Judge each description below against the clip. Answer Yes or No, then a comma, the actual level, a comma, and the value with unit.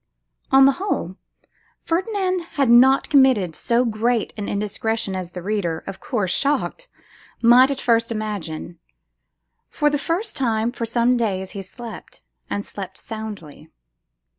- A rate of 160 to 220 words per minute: No, average, 140 wpm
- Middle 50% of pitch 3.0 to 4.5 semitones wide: No, average, 5.0 semitones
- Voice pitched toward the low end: No, high, 230 Hz